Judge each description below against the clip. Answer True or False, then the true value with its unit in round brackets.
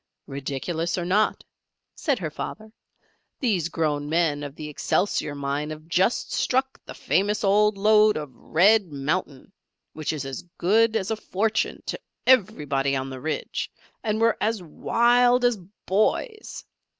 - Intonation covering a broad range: True (6.5 semitones)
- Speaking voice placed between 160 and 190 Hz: True (185 Hz)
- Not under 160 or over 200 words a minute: False (145 wpm)